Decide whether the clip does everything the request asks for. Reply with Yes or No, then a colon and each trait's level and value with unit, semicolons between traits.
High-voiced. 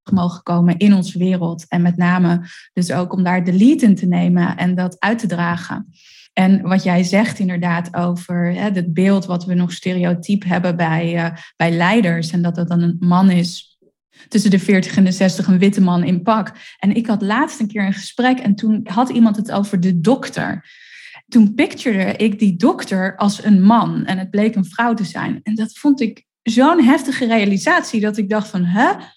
Yes: high, 195 Hz